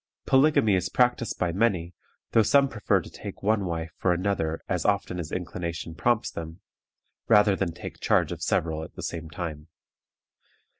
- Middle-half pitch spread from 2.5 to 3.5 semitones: No, average, 4.2 semitones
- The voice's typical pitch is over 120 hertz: No, very low, 90 Hz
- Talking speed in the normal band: Yes, average, 165 wpm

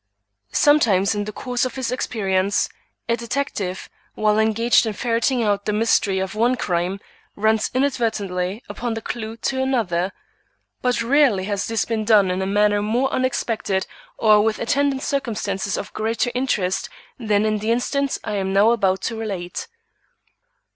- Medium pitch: No, high, 220 Hz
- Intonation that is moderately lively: Yes, average, 3.4 semitones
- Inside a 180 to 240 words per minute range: No, average, 155 wpm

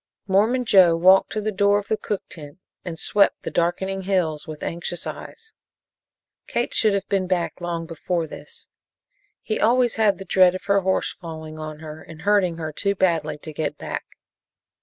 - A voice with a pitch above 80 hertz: Yes, medium, 185 Hz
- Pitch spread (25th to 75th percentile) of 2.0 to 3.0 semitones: No, average, 3.5 semitones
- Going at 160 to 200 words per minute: Yes, average, 180 wpm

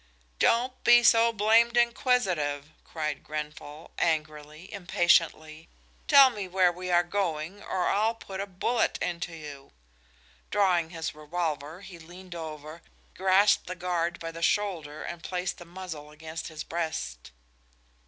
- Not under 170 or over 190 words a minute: No, slow, 135 wpm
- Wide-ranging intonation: No, average, 4.0 semitones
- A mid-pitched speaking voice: Yes, medium, 175 Hz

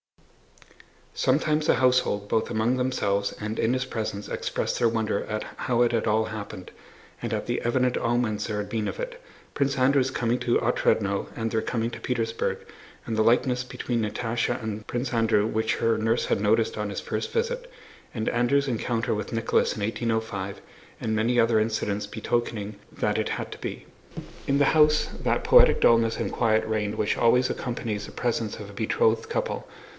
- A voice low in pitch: Yes, low, 115 Hz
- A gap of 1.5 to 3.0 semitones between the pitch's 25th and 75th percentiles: Yes, narrow, 2.4 semitones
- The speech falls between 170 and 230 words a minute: Yes, average, 180 wpm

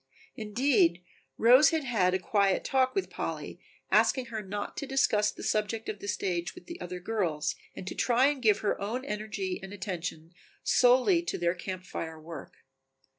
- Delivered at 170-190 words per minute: Yes, average, 175 wpm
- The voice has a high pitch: Yes, high, 210 Hz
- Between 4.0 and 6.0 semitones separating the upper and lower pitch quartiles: Yes, average, 5.3 semitones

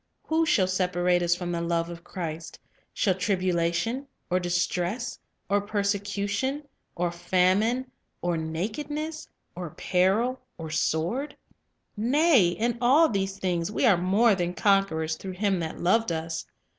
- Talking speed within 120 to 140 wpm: Yes, slow, 135 wpm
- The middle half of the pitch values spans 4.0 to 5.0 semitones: Yes, average, 4.6 semitones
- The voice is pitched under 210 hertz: Yes, medium, 185 Hz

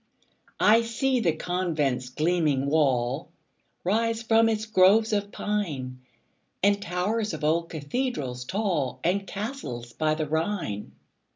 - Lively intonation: Yes, wide, 6.9 semitones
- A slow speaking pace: Yes, slow, 120 wpm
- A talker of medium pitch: Yes, medium, 180 Hz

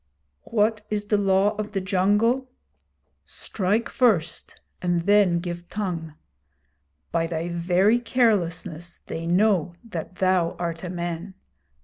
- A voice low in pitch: No, medium, 185 Hz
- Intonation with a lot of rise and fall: No, average, 3.4 semitones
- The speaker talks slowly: Yes, slow, 120 wpm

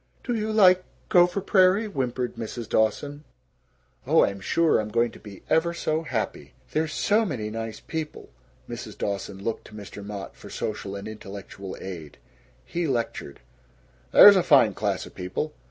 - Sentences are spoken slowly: No, average, 160 wpm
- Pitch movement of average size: No, wide, 8.7 semitones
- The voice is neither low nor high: No, low, 120 Hz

